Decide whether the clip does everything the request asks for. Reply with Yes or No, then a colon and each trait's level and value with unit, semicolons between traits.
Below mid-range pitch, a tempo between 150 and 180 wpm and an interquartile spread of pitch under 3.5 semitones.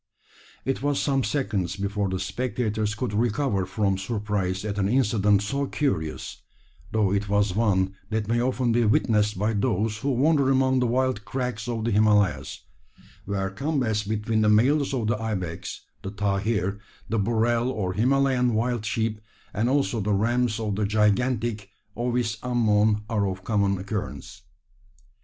Yes: low, 110 Hz; average, 155 wpm; average, 3.1 semitones